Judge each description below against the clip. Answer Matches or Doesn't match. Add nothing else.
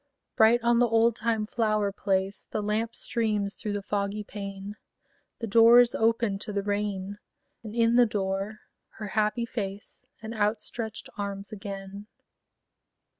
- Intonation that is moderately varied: Doesn't match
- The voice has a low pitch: Doesn't match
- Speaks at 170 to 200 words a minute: Doesn't match